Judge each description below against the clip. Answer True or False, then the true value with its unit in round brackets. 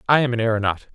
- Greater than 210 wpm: True (255 wpm)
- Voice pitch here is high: False (115 Hz)